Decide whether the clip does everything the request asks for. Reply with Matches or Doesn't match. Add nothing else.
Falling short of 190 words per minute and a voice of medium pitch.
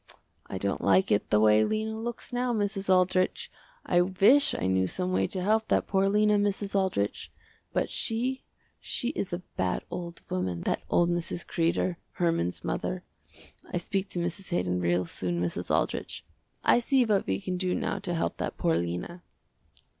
Matches